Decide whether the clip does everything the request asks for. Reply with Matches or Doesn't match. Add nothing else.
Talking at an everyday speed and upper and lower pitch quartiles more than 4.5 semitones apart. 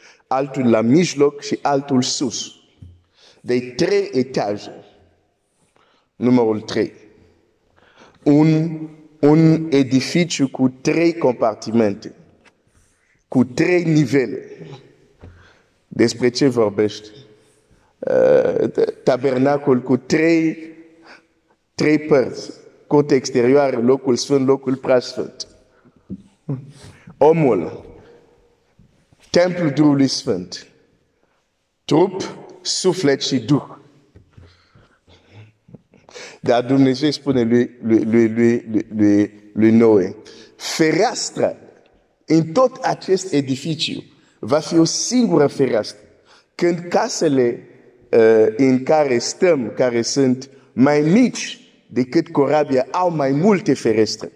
Doesn't match